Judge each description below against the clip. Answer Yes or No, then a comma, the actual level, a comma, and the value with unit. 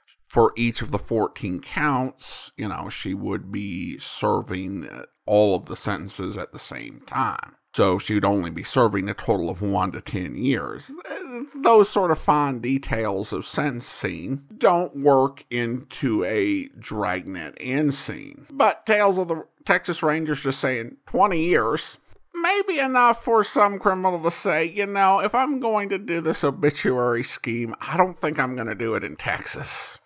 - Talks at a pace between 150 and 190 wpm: Yes, average, 170 wpm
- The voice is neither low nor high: Yes, medium, 150 Hz